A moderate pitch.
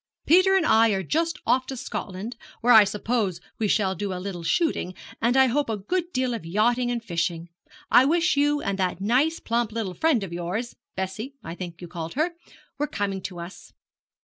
No: high, 220 Hz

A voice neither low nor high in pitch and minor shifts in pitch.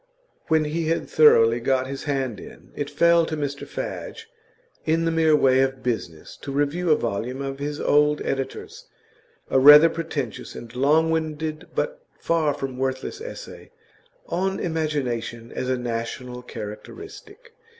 No: medium, 145 Hz; average, 4.0 semitones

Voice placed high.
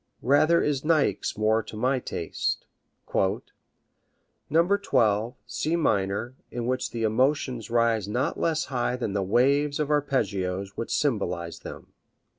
No: low, 120 Hz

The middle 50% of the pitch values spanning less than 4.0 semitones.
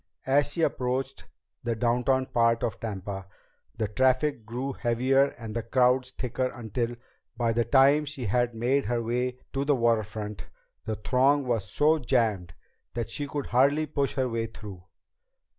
Yes: average, 2.8 semitones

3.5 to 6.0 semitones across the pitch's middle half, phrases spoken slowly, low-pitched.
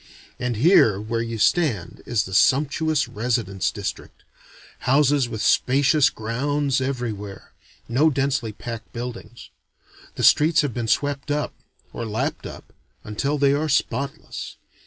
Yes: average, 4.3 semitones; slow, 130 wpm; low, 125 Hz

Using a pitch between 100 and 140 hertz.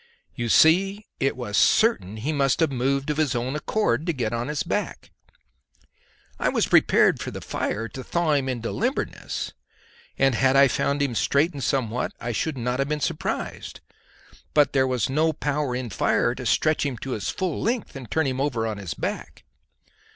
Yes: low, 135 Hz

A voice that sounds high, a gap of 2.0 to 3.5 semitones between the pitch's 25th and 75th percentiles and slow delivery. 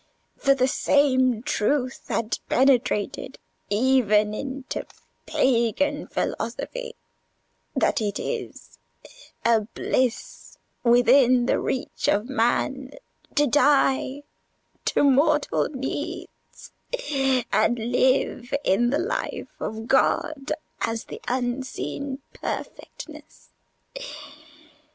Yes: very high, 260 Hz; average, 2.8 semitones; slow, 85 wpm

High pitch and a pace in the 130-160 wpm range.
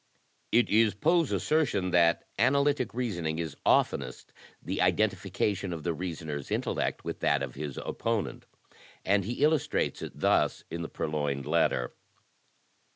No: very low, 90 Hz; average, 140 wpm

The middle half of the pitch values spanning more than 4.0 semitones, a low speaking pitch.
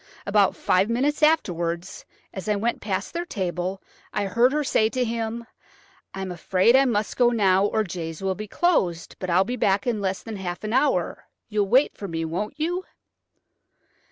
No: average, 4.4 semitones; high, 205 Hz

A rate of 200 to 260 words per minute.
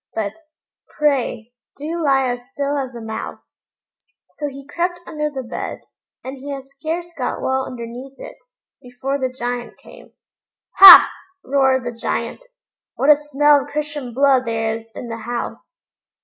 No: average, 155 wpm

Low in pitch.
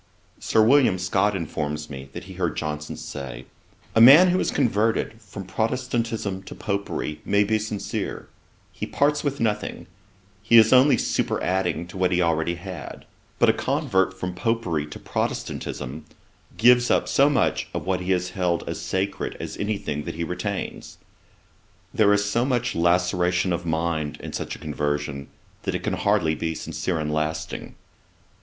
Yes: very low, 95 Hz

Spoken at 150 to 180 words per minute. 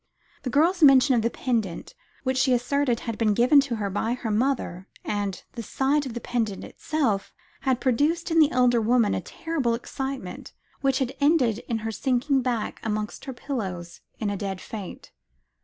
Yes: average, 175 wpm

